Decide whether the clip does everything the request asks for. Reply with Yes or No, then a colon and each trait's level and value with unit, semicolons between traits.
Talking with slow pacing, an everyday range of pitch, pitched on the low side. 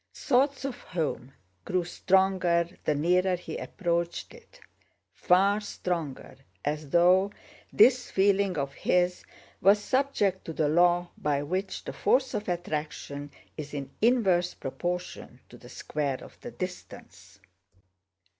No: slow, 125 wpm; average, 4.0 semitones; medium, 180 Hz